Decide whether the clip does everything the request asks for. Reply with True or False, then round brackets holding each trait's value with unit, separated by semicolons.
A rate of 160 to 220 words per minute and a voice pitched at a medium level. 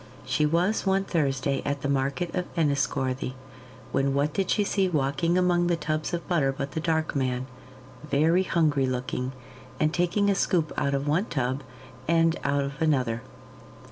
True (170 wpm; 150 Hz)